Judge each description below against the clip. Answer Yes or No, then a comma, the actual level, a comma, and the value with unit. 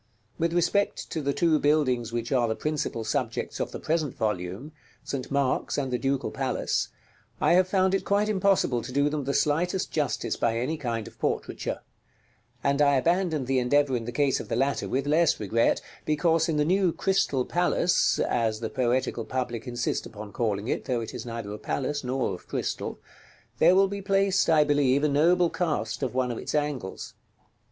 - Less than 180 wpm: No, average, 195 wpm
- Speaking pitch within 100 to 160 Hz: Yes, medium, 140 Hz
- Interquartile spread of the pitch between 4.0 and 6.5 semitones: Yes, average, 5.3 semitones